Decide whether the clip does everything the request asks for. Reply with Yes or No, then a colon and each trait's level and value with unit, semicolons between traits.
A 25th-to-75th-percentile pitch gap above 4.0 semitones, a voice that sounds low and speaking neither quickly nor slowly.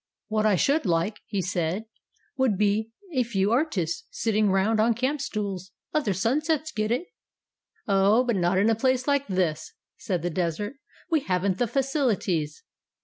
No: average, 5.3 semitones; high, 215 Hz; average, 160 wpm